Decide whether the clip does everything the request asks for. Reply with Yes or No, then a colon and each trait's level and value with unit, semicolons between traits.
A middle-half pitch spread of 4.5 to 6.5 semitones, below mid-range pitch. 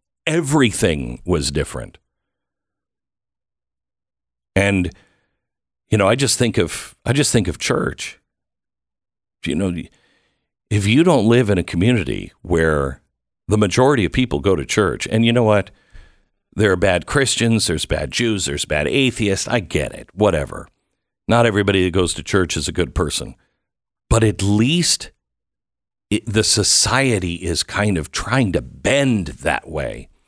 Yes: wide, 5.6 semitones; low, 105 Hz